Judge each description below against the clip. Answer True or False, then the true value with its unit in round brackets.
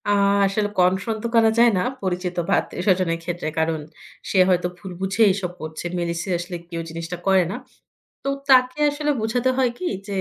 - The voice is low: False (185 Hz)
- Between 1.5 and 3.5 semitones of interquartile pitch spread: False (4.2 semitones)